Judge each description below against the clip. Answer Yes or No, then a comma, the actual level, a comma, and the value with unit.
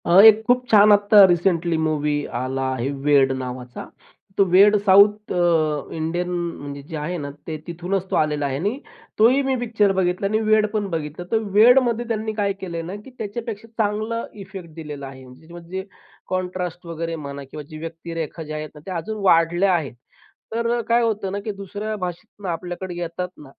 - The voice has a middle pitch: Yes, medium, 180 Hz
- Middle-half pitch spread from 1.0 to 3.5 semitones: No, average, 4.8 semitones